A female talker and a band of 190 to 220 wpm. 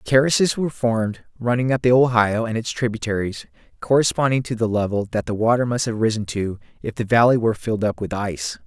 No: male; average, 200 wpm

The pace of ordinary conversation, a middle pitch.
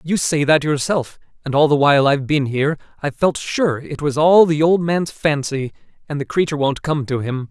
No: fast, 225 wpm; medium, 150 Hz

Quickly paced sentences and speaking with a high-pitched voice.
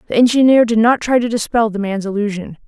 Yes: fast, 225 wpm; high, 220 Hz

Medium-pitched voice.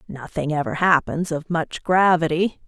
Yes: medium, 165 Hz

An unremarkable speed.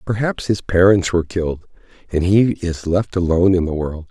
Yes: average, 190 wpm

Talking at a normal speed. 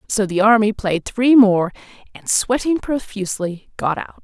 Yes: average, 155 wpm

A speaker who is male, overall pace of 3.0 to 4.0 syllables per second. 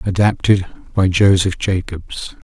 Yes: male; 3.9 syllables/s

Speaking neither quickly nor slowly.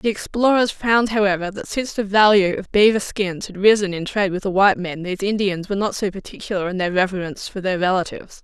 No: fast, 220 wpm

